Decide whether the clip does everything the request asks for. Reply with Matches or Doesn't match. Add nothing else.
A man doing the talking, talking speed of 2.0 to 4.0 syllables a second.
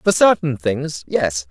Matches